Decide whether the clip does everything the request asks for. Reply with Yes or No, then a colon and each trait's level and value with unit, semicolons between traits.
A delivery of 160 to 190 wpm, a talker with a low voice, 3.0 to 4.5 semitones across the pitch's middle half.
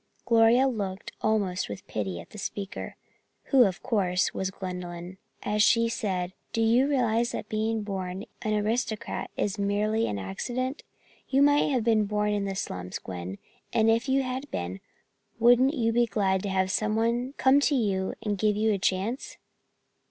No: average, 170 wpm; high, 215 Hz; average, 3.8 semitones